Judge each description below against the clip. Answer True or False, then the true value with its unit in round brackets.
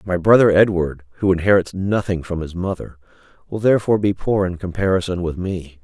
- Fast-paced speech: False (175 wpm)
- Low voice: True (90 Hz)